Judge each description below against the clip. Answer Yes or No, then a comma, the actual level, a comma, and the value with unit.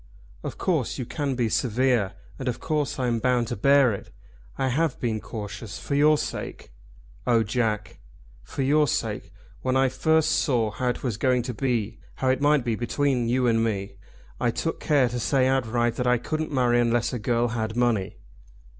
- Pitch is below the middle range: Yes, low, 125 Hz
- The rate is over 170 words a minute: Yes, average, 190 wpm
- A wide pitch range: No, average, 2.7 semitones